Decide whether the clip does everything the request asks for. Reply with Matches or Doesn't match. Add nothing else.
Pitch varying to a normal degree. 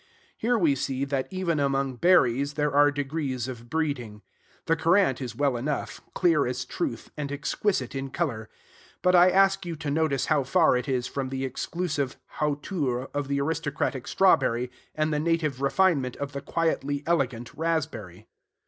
Matches